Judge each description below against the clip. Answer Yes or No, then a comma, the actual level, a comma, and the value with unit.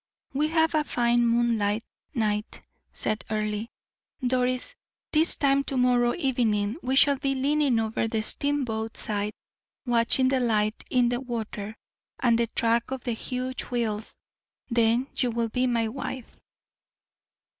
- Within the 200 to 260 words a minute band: No, average, 140 wpm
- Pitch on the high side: Yes, high, 240 Hz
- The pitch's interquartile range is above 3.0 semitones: No, average, 2.7 semitones